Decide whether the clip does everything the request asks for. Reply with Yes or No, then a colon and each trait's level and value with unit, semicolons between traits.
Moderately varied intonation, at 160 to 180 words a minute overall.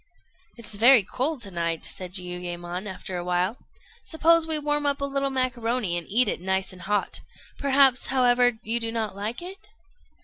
No: wide, 6.6 semitones; average, 175 wpm